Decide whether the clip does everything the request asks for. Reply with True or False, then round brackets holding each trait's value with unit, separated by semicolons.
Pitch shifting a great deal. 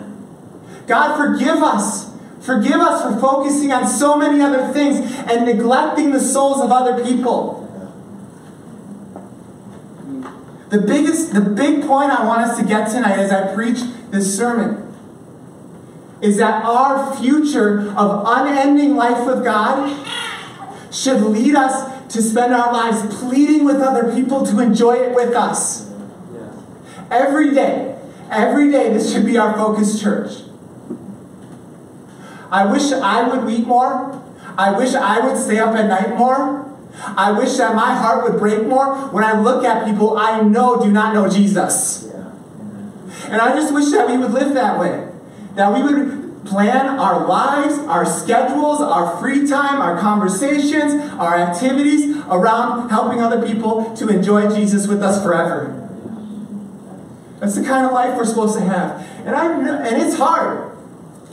False (4.0 semitones)